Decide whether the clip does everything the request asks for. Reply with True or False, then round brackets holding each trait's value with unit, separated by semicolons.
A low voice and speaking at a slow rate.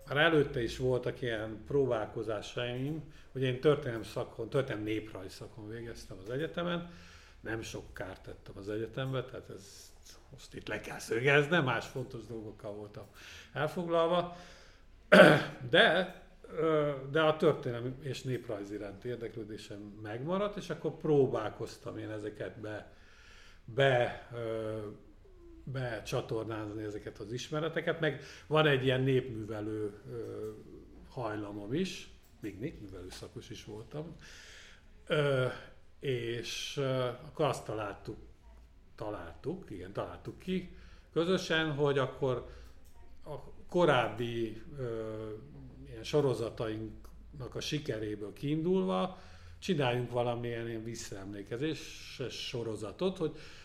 True (120 Hz; 100 wpm)